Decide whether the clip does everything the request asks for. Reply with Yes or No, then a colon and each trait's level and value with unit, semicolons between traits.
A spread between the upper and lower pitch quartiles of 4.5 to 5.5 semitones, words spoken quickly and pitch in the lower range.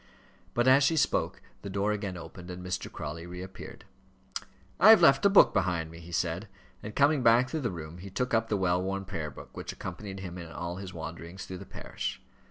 Yes: average, 4.8 semitones; fast, 215 wpm; very low, 95 Hz